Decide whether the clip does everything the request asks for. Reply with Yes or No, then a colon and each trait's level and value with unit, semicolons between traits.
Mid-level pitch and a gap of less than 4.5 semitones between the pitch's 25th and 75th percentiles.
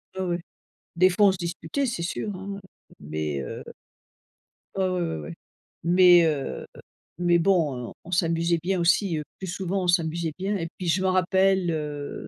Yes: medium, 175 Hz; narrow, 2.4 semitones